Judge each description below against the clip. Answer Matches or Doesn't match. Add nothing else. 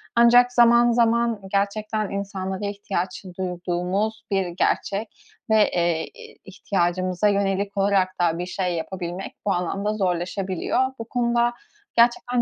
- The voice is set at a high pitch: Matches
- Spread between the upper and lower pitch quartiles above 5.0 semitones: Doesn't match